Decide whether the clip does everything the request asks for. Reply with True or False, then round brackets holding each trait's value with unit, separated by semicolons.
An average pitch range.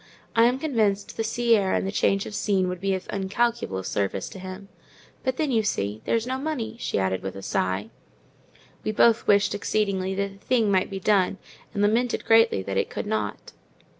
True (3.5 semitones)